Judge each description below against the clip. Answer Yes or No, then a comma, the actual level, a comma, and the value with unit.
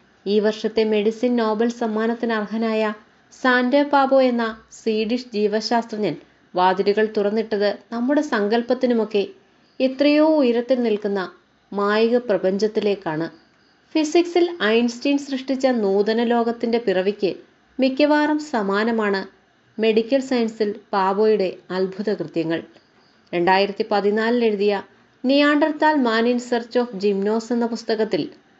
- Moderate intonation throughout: Yes, average, 3.3 semitones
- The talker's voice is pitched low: No, high, 225 Hz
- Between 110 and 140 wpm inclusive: No, average, 90 wpm